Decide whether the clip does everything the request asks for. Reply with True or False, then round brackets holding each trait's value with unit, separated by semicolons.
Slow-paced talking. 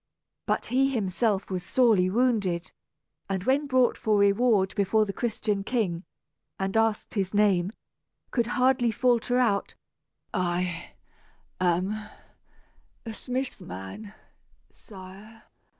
True (110 wpm)